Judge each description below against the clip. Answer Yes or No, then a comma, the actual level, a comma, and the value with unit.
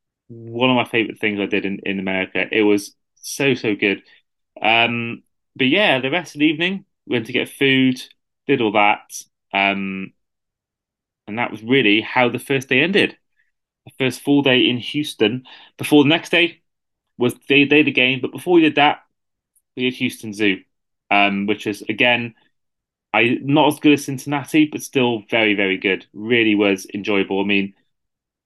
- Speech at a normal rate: Yes, average, 180 wpm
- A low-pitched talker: Yes, low, 120 Hz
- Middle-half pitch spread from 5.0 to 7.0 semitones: Yes, average, 5.3 semitones